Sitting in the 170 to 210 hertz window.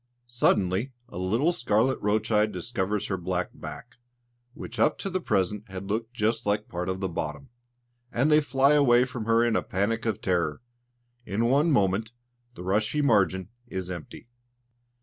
No: low, 110 Hz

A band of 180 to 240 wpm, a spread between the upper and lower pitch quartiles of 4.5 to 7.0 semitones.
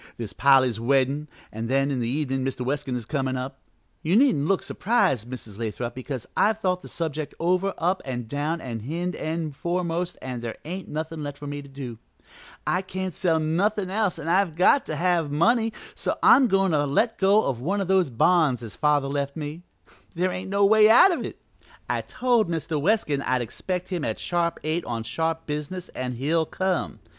Yes: average, 200 wpm; average, 5.3 semitones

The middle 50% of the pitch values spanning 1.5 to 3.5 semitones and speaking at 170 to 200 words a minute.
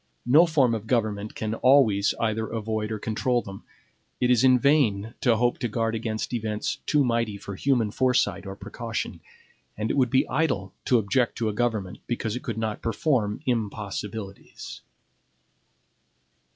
No: average, 2.8 semitones; average, 160 wpm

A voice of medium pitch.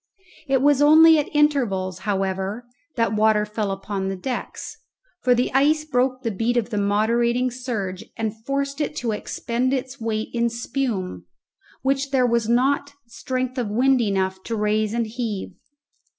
No: high, 235 Hz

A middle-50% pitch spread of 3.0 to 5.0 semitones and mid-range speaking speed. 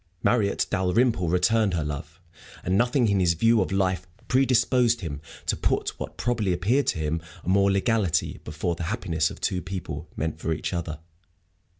No: wide, 5.4 semitones; average, 175 wpm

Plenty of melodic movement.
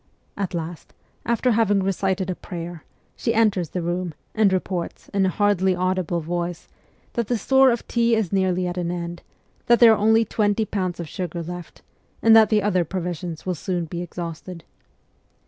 No: average, 3.3 semitones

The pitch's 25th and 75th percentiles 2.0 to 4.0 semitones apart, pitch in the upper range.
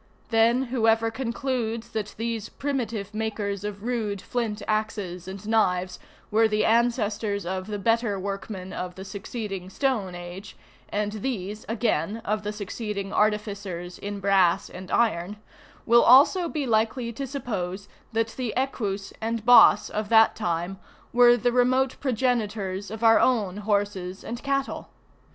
Yes: average, 2.9 semitones; high, 215 Hz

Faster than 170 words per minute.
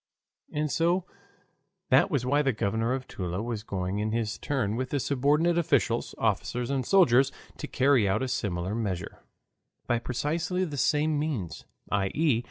No: average, 165 wpm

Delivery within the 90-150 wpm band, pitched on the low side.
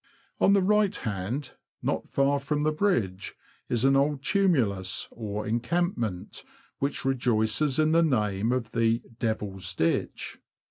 Yes: average, 140 wpm; low, 125 Hz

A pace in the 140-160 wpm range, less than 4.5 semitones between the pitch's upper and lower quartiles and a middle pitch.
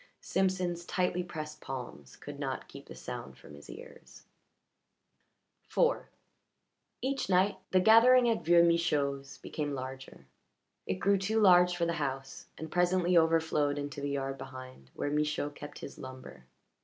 No: average, 145 wpm; average, 4.8 semitones; medium, 155 Hz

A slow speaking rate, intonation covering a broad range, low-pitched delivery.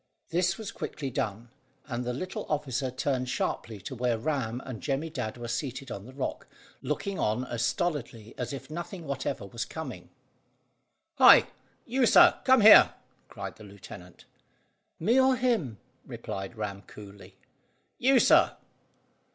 No: average, 145 wpm; wide, 6.7 semitones; low, 130 Hz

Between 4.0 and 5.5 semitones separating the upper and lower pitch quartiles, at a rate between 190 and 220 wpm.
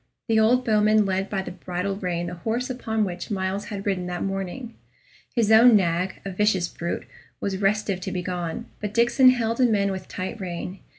No: average, 3.2 semitones; average, 195 wpm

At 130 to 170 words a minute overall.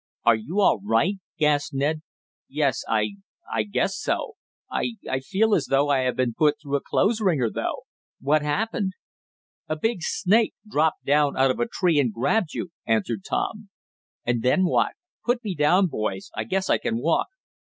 No: average, 180 wpm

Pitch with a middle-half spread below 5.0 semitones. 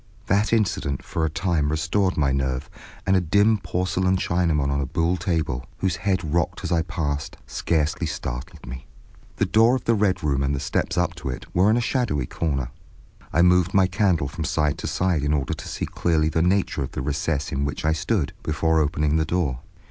Yes: average, 4.2 semitones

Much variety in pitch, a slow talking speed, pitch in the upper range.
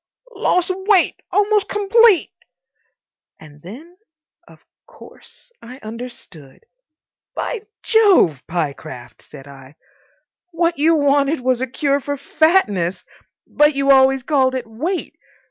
Yes: wide, 8.3 semitones; slow, 110 wpm; very high, 275 Hz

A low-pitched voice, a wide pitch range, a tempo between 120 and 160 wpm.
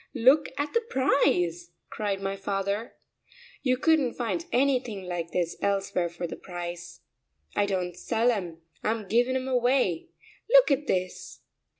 No: high, 205 Hz; wide, 6.4 semitones; average, 140 wpm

